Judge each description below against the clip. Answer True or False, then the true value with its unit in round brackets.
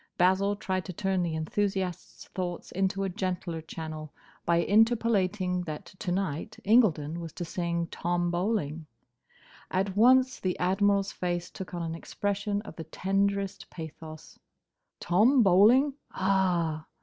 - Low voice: False (185 Hz)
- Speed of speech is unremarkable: False (130 wpm)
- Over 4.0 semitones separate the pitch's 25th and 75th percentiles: False (2.9 semitones)